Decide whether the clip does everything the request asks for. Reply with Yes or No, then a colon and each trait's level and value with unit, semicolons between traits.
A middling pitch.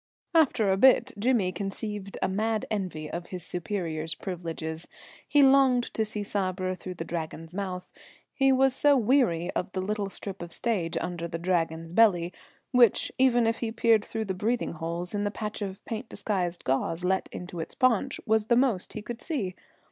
No: high, 195 Hz